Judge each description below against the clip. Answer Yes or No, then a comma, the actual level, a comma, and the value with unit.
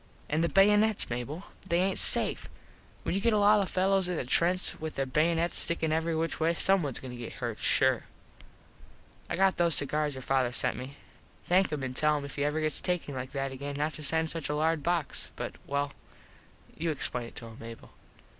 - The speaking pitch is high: No, medium, 155 Hz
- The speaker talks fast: Yes, fast, 220 wpm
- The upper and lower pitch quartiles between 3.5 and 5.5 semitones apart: Yes, average, 4.0 semitones